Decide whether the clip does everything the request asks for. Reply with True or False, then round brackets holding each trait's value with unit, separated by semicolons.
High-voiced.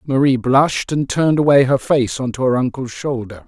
False (130 Hz)